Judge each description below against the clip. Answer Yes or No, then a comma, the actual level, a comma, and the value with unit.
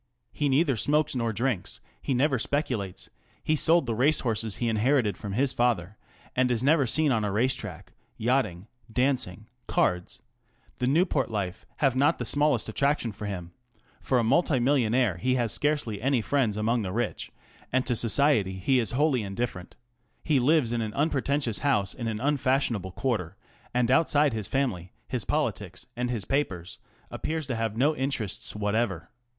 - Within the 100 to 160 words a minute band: No, average, 170 wpm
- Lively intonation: No, average, 4.6 semitones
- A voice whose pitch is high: No, low, 120 Hz